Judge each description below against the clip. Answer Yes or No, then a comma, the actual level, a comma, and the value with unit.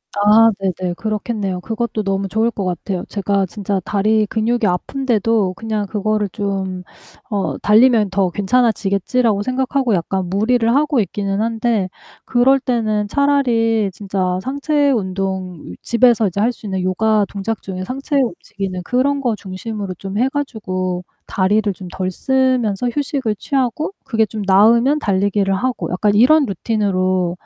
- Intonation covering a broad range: No, average, 3.7 semitones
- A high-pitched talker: Yes, high, 210 Hz